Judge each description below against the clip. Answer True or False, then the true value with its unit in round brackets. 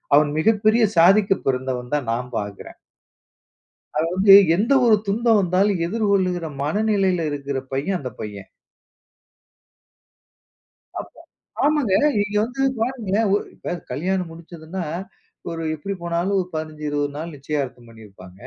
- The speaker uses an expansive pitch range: True (6.0 semitones)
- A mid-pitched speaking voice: True (170 Hz)